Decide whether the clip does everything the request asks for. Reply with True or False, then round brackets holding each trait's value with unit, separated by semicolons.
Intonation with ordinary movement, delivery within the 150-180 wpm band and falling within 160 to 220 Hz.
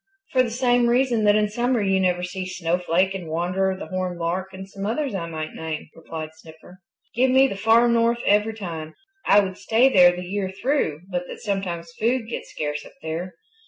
False (4.6 semitones; 200 wpm; 190 Hz)